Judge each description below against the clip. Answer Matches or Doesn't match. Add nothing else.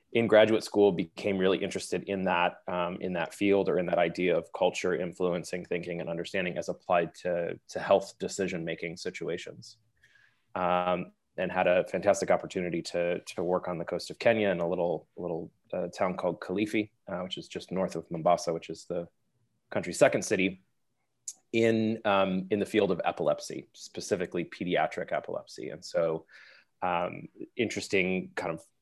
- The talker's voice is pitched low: Matches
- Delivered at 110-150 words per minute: Doesn't match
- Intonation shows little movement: Doesn't match